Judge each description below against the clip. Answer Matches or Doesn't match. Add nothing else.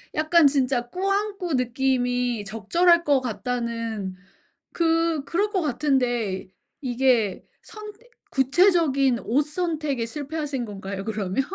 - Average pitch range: Doesn't match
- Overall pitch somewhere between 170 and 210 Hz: Doesn't match